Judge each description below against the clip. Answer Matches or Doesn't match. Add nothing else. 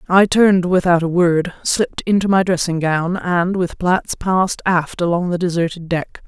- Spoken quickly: Doesn't match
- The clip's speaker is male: Doesn't match